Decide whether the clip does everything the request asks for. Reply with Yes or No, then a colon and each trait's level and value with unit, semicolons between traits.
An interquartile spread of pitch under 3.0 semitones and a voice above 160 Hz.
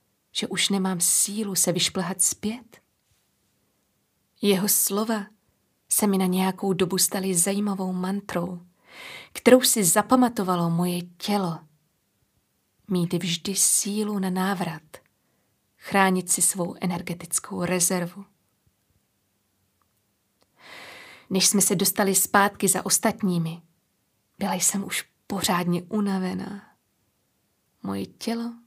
Yes: narrow, 2.5 semitones; high, 190 Hz